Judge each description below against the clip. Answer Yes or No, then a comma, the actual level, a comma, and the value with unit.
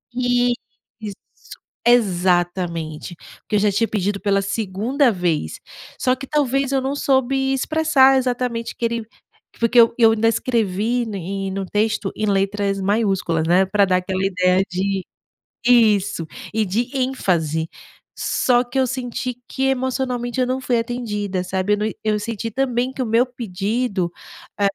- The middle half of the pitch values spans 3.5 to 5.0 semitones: Yes, average, 4.4 semitones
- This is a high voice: Yes, high, 220 Hz